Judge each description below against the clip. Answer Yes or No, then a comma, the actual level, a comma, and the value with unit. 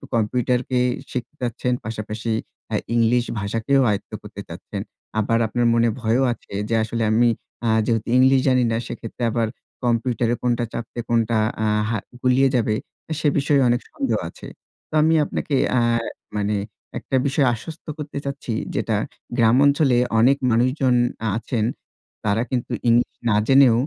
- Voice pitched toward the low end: Yes, low, 120 Hz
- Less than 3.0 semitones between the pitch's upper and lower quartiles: Yes, narrow, 2.5 semitones